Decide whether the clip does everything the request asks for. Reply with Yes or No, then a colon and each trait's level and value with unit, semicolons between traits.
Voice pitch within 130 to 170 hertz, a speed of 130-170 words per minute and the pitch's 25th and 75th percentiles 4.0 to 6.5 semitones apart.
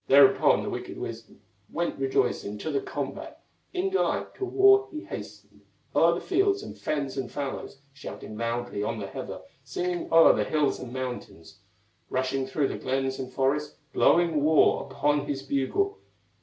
Yes: medium, 140 Hz; average, 160 wpm; average, 4.5 semitones